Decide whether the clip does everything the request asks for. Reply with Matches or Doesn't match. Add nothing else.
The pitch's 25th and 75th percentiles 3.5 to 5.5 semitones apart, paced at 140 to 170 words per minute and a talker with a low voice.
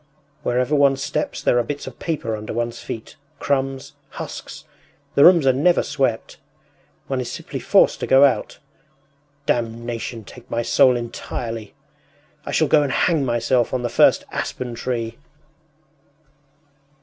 Doesn't match